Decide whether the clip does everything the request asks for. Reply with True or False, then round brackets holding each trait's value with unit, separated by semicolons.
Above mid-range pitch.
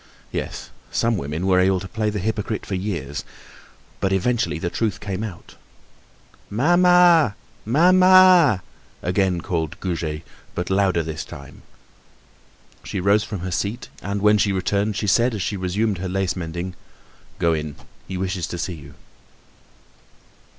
False (95 Hz)